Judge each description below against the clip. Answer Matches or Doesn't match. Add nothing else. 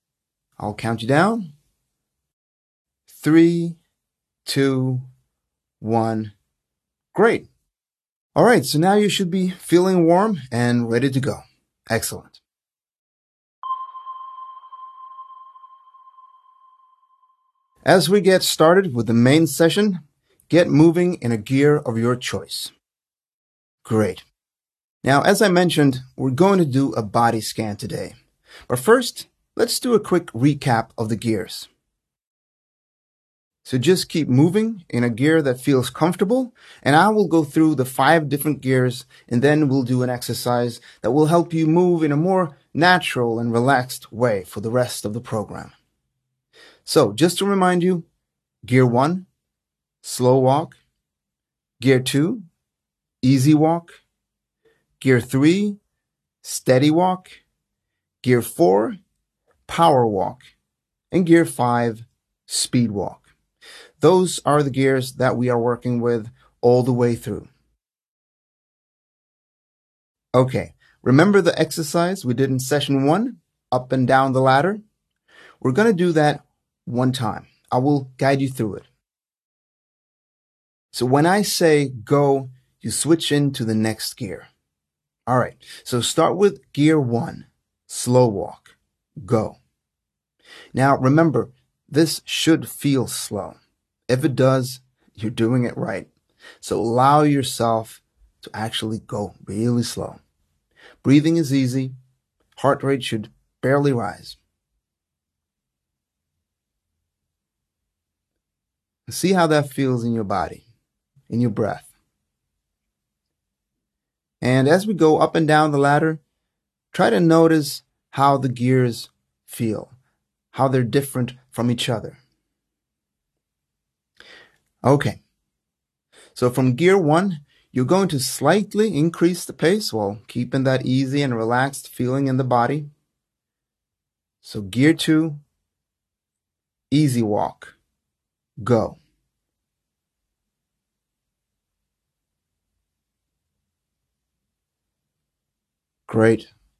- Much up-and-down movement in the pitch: Matches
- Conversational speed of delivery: Doesn't match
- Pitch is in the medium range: Doesn't match